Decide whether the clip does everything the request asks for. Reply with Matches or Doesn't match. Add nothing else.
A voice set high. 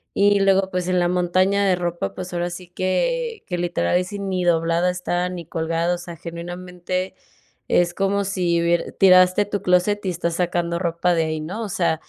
Doesn't match